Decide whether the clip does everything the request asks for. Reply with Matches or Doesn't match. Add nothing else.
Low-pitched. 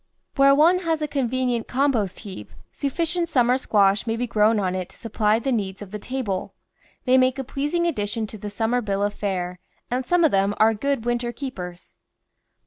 Doesn't match